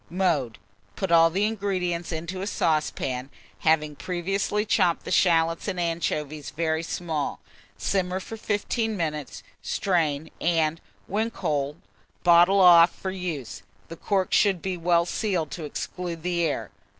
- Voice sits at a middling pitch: Yes, medium, 170 Hz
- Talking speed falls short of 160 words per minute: Yes, average, 140 wpm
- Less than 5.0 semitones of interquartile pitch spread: Yes, average, 2.9 semitones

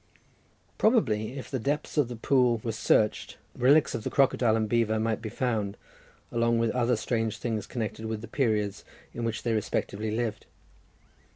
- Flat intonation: Yes, narrow, 2.3 semitones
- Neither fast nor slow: Yes, average, 175 wpm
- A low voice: Yes, low, 115 Hz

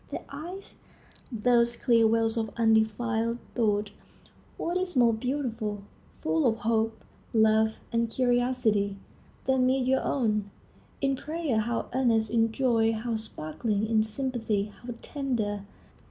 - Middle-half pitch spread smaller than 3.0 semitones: Yes, narrow, 2.4 semitones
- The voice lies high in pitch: Yes, high, 230 Hz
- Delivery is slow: Yes, slow, 125 wpm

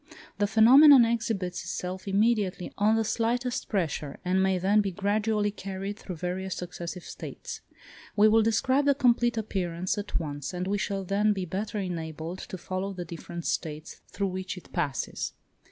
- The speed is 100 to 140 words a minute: No, average, 165 wpm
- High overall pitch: Yes, high, 195 Hz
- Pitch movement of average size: Yes, average, 3.4 semitones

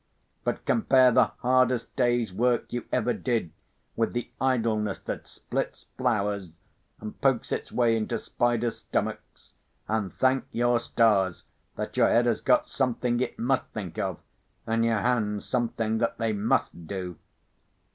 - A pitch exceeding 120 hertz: No, low, 115 Hz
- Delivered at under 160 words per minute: Yes, average, 145 wpm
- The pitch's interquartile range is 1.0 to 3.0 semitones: Yes, narrow, 2.5 semitones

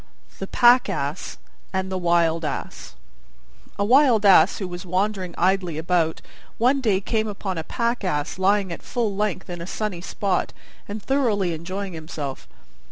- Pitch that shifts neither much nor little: Yes, average, 3.6 semitones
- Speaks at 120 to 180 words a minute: Yes, average, 160 wpm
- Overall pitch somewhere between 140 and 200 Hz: Yes, high, 190 Hz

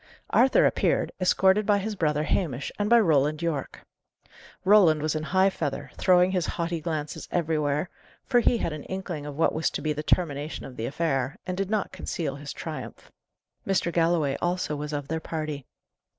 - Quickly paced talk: No, average, 180 wpm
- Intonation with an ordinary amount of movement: Yes, average, 3.9 semitones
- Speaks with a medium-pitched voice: Yes, medium, 160 Hz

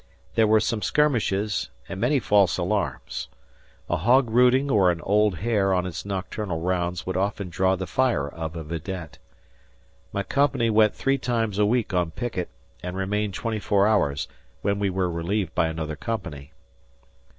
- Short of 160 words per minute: No, average, 165 wpm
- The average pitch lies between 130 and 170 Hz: No, low, 100 Hz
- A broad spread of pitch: No, average, 3.8 semitones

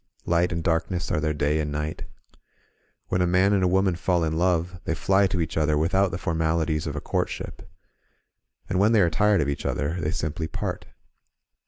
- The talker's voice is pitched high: No, very low, 85 Hz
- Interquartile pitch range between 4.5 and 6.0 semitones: No, average, 2.9 semitones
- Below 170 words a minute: No, fast, 205 wpm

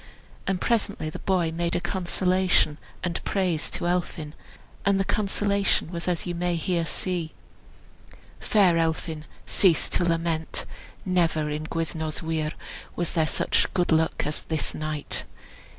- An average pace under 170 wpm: Yes, average, 140 wpm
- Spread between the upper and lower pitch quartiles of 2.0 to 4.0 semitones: Yes, narrow, 2.4 semitones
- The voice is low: No, medium, 170 Hz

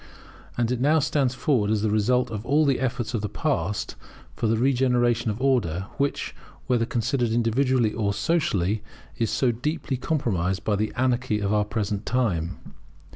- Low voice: Yes, low, 120 Hz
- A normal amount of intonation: Yes, average, 3.6 semitones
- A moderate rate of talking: Yes, average, 170 wpm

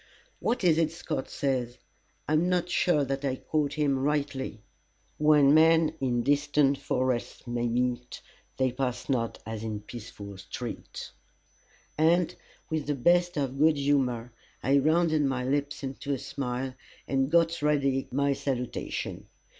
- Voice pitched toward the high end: No, medium, 140 Hz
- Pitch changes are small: No, average, 3.3 semitones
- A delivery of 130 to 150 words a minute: Yes, average, 140 wpm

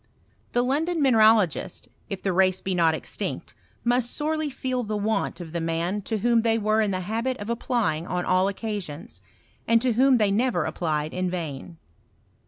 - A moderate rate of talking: Yes, average, 180 wpm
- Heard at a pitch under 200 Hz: No, high, 210 Hz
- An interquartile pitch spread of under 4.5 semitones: No, average, 5.1 semitones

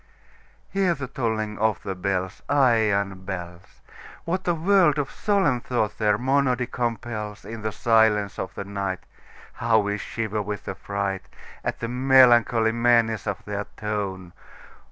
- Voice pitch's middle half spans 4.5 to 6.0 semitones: No, average, 3.6 semitones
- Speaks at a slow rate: Yes, slow, 120 wpm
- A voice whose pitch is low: Yes, low, 110 Hz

